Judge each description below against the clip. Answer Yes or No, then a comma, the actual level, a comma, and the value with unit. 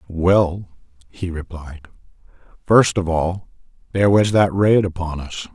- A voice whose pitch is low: Yes, very low, 90 Hz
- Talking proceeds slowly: Yes, slow, 130 wpm